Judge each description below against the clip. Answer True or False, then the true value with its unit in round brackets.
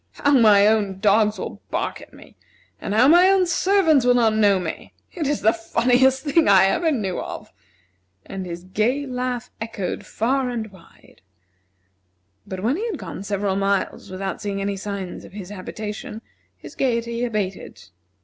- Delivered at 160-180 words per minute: True (170 wpm)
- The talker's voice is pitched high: True (220 Hz)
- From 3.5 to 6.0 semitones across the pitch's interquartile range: True (4.5 semitones)